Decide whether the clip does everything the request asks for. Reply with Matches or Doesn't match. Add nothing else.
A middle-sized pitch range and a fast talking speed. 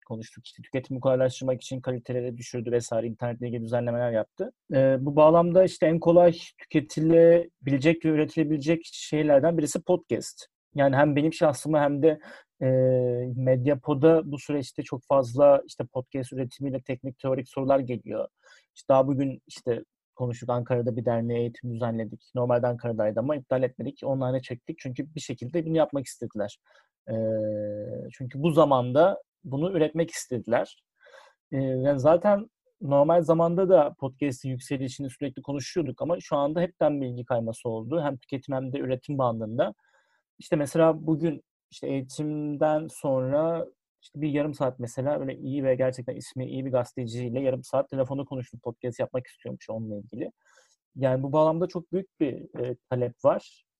Matches